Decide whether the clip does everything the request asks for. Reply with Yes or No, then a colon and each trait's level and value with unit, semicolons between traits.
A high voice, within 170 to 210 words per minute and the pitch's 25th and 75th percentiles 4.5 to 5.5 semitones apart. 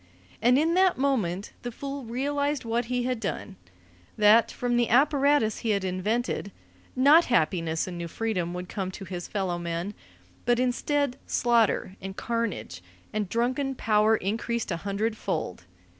No: high, 225 Hz; average, 150 wpm; average, 4.8 semitones